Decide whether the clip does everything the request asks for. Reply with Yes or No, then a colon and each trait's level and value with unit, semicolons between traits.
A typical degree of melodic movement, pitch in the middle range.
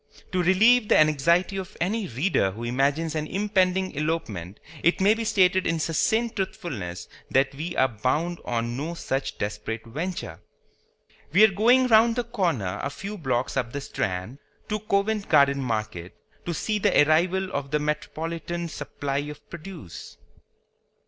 No: wide, 6.2 semitones; medium, 160 Hz